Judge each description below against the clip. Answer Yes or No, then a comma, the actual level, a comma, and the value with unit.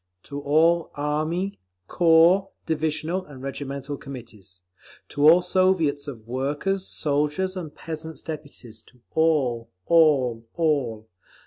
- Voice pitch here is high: No, medium, 150 Hz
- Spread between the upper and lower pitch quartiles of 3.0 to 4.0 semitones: Yes, average, 3.4 semitones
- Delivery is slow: Yes, slow, 110 wpm